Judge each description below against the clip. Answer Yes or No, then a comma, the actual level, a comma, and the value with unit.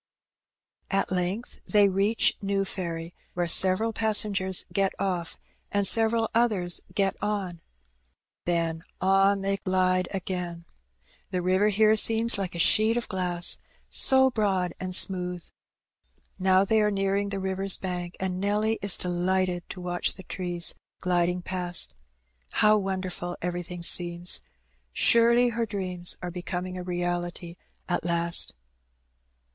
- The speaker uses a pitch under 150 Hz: No, medium, 185 Hz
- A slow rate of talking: Yes, slow, 130 wpm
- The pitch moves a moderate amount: No, narrow, 2.3 semitones